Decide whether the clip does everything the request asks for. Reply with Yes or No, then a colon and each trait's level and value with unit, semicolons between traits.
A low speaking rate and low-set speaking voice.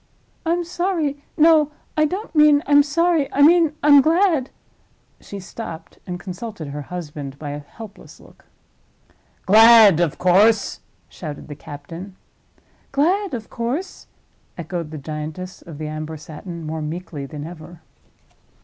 No: slow, 130 wpm; high, 190 Hz